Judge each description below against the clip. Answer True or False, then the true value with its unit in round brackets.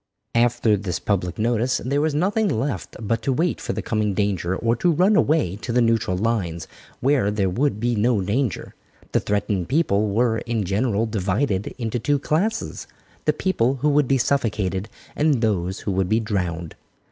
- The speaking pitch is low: True (115 Hz)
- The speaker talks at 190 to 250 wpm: False (180 wpm)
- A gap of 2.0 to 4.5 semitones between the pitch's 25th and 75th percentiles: False (5.2 semitones)